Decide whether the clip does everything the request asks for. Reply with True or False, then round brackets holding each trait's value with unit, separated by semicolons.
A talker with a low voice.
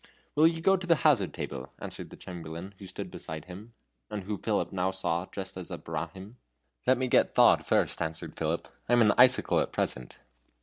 True (95 Hz)